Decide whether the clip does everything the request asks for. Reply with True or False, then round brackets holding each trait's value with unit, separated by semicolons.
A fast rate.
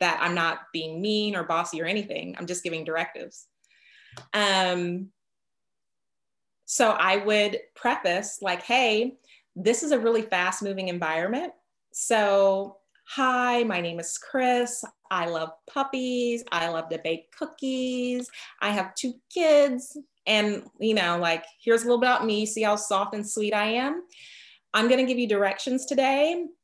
False (155 wpm)